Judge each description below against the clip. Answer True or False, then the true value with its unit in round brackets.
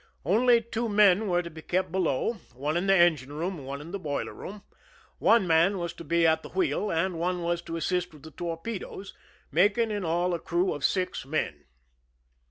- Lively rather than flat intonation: False (3.3 semitones)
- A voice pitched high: False (175 Hz)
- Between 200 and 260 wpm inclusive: True (205 wpm)